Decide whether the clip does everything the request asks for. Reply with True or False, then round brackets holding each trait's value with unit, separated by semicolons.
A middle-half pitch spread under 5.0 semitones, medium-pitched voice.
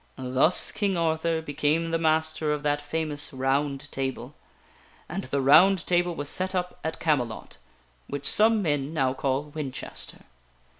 True (3.2 semitones; 150 Hz)